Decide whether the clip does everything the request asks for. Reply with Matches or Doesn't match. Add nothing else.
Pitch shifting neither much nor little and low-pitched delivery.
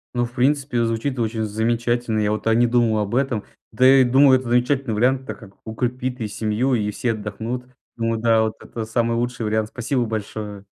Doesn't match